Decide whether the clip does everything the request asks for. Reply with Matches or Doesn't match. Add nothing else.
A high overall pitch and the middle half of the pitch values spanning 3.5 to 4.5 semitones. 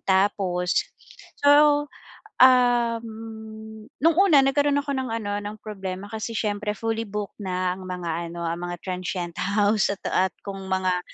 Matches